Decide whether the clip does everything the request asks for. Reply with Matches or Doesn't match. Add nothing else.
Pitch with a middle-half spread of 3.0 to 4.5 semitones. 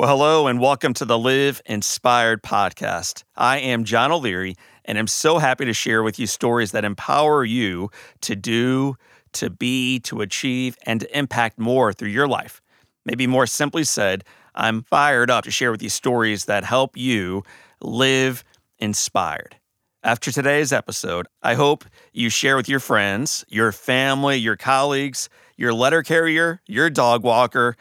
Matches